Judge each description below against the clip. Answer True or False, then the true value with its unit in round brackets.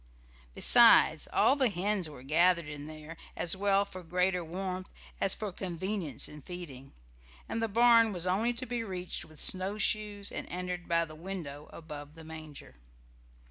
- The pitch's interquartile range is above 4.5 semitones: False (4.0 semitones)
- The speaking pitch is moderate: True (180 Hz)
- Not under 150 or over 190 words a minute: True (160 wpm)